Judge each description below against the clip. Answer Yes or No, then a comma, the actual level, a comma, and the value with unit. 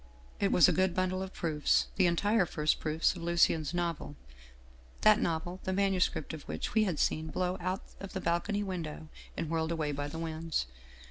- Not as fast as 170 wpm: No, average, 195 wpm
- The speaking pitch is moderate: Yes, medium, 170 Hz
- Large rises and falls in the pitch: No, average, 2.9 semitones